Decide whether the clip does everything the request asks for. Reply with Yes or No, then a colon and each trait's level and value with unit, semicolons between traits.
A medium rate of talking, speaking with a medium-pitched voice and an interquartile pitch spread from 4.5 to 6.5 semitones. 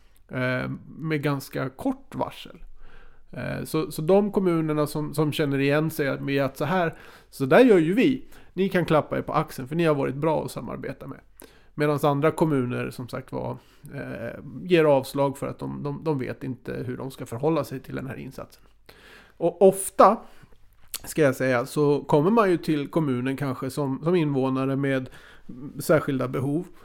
No: average, 165 wpm; medium, 145 Hz; average, 3.3 semitones